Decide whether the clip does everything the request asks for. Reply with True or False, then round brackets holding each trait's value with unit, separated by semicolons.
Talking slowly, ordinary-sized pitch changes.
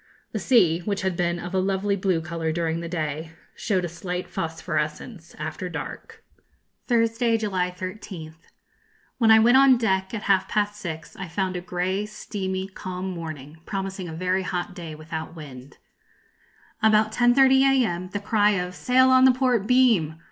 False (165 wpm; 4.1 semitones)